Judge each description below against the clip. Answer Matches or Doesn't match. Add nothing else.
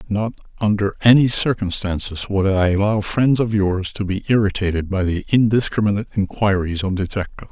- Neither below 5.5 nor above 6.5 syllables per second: Matches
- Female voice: Doesn't match